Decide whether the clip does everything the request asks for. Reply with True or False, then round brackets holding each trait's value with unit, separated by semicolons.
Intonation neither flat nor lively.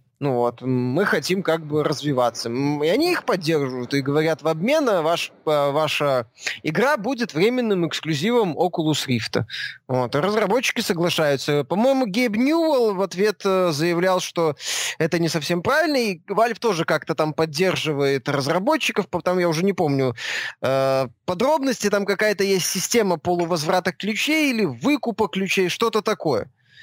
False (6.2 semitones)